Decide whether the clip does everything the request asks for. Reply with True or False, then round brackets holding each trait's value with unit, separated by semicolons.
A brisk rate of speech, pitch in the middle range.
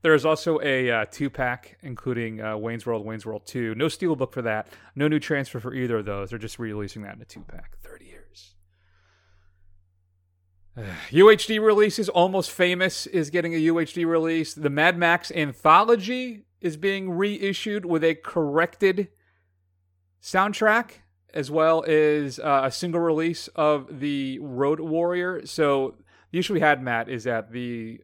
False (165 wpm; 145 Hz)